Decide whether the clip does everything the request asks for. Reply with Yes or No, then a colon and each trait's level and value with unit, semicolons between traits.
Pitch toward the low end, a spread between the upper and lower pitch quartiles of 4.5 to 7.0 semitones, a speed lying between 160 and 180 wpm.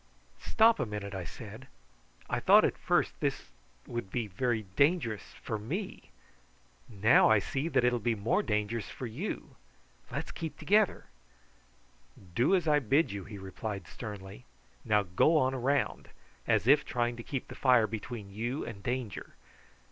Yes: low, 120 Hz; average, 4.9 semitones; average, 165 wpm